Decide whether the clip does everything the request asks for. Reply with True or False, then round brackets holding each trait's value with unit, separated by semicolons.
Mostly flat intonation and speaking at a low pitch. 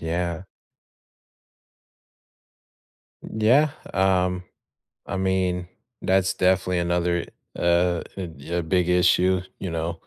True (1.4 semitones; 90 Hz)